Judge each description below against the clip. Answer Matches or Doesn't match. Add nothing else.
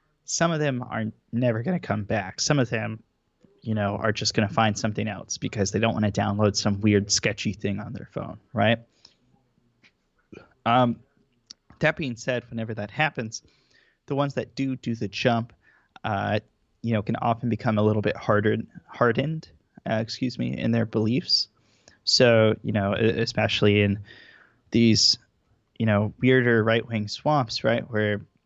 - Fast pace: Doesn't match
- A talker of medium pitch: Doesn't match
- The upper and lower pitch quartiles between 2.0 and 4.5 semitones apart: Matches